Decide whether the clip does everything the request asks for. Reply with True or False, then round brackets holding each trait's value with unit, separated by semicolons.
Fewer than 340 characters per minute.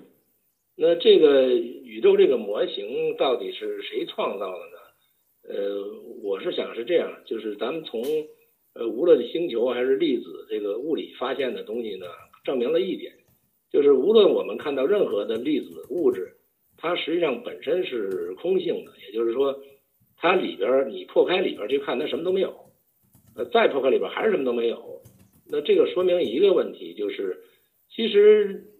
True (260 characters per minute)